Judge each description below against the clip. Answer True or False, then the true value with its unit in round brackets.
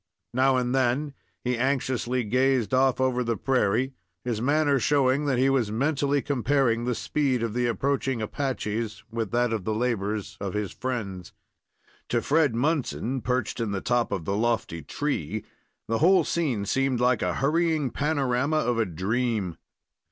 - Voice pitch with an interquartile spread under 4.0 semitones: True (3.3 semitones)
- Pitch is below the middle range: True (125 Hz)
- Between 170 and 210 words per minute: False (160 wpm)